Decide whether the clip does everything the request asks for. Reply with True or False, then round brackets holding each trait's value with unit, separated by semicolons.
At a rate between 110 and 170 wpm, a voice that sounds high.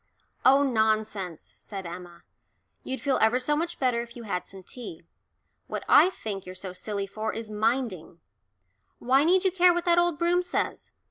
False (180 wpm; 230 Hz)